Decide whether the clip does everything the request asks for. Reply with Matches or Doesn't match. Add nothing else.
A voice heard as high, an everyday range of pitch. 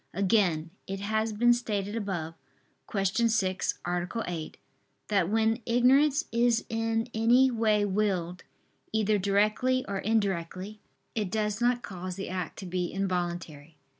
Matches